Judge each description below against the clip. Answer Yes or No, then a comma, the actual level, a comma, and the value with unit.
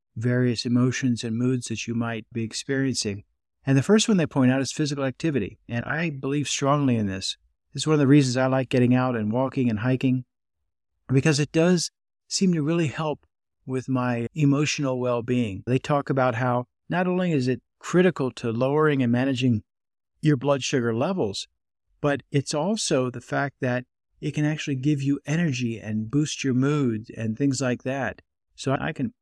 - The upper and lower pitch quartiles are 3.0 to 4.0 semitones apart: Yes, average, 3.6 semitones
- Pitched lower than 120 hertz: No, low, 130 Hz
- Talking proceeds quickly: No, average, 185 wpm